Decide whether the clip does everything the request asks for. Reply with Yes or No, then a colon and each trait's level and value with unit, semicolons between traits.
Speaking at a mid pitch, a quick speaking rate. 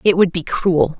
Yes: medium, 175 Hz; fast, 240 wpm